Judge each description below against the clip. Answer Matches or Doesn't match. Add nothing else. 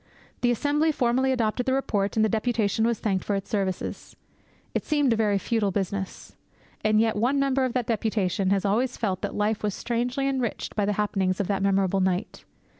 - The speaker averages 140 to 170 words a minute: Doesn't match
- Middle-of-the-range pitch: Doesn't match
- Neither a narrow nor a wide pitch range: Matches